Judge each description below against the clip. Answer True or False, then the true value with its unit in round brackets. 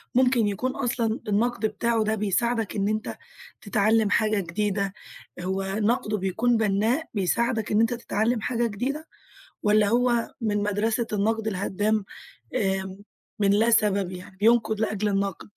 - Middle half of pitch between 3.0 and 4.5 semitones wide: False (2.5 semitones)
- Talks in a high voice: True (215 Hz)